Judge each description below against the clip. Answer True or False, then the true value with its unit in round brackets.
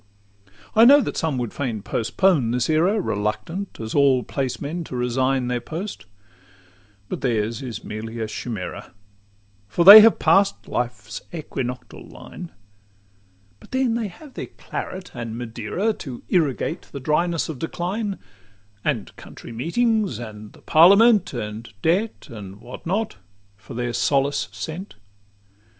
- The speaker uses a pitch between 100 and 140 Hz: True (135 Hz)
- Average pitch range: False (8.0 semitones)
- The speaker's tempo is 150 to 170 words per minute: False (140 wpm)